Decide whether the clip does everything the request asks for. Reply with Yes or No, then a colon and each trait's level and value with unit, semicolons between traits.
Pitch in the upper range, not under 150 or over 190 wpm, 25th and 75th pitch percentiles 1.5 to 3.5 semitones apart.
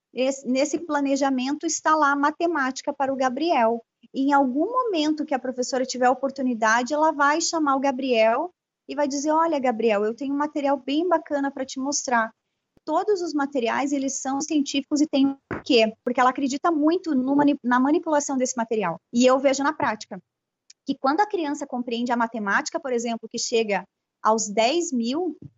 Yes: very high, 275 Hz; fast, 185 wpm; average, 3.2 semitones